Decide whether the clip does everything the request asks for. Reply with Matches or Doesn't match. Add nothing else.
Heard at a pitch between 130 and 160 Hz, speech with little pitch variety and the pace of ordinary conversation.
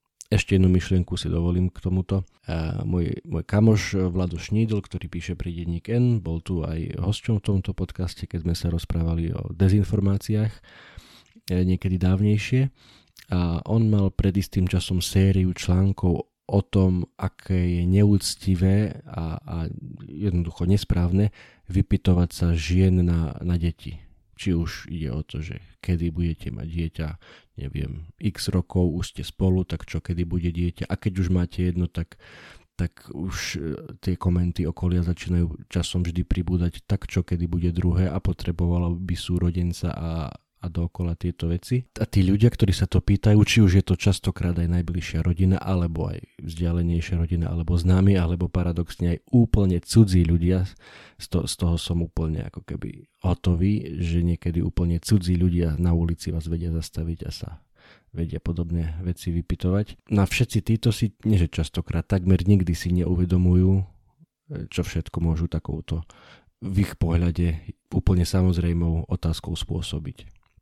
Doesn't match